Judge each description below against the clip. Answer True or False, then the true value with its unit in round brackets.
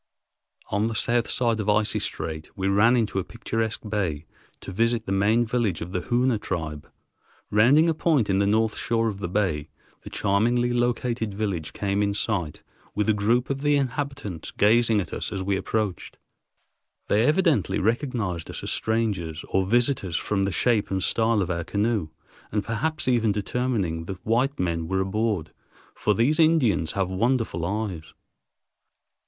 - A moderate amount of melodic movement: True (3.8 semitones)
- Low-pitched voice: True (105 Hz)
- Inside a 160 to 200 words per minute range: True (170 wpm)